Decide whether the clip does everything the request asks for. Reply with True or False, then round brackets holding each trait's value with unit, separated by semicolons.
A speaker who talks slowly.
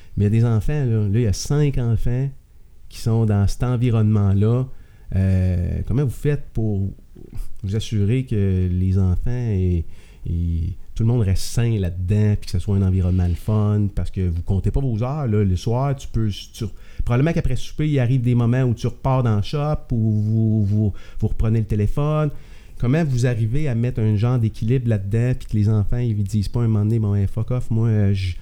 False (220 wpm)